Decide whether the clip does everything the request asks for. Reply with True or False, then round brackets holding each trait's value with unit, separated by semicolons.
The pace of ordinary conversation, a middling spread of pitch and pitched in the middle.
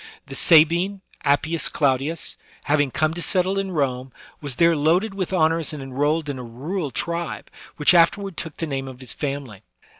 True (175 wpm; 3.7 semitones; 155 Hz)